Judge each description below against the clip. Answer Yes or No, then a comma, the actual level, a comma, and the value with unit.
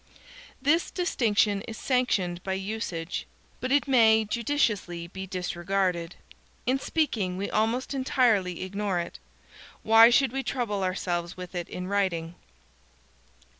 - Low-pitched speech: No, high, 205 Hz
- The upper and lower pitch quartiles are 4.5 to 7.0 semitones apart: Yes, average, 5.1 semitones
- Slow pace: Yes, slow, 125 wpm